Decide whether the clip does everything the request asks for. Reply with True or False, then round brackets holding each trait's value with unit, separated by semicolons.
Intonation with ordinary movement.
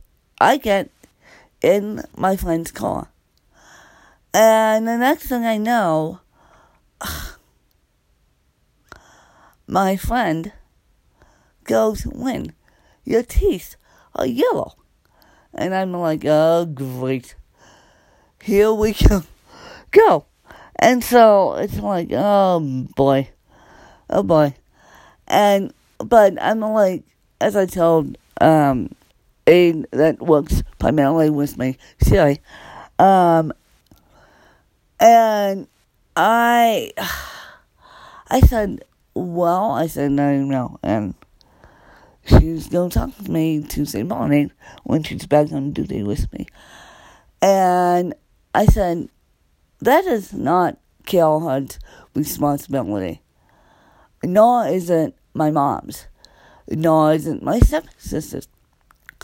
False (6.6 semitones)